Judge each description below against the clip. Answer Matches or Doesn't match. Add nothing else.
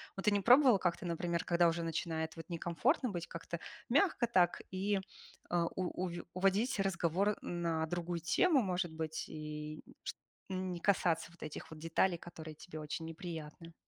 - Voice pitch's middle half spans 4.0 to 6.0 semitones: Doesn't match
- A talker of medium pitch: Matches